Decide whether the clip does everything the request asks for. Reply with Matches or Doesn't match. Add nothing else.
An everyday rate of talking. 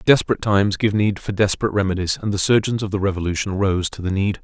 Doesn't match